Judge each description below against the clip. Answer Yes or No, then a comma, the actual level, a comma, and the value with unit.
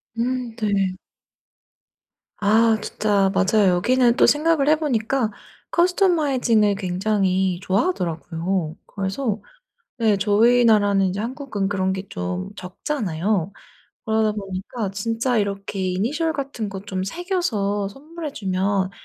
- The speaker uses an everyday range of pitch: Yes, average, 4.4 semitones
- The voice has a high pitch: Yes, high, 210 Hz